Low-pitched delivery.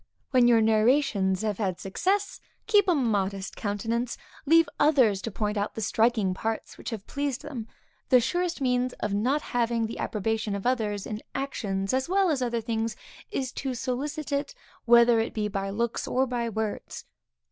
No: high, 235 Hz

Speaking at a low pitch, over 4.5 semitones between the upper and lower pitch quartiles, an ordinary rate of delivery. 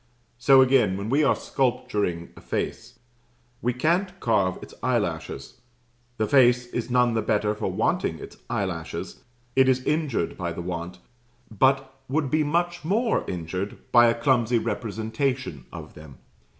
Yes: low, 120 Hz; average, 5.1 semitones; average, 150 wpm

